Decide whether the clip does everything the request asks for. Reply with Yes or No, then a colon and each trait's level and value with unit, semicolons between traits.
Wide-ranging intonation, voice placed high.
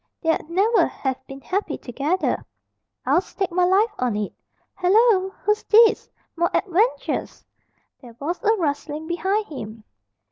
Yes: wide, 6.2 semitones; very high, 355 Hz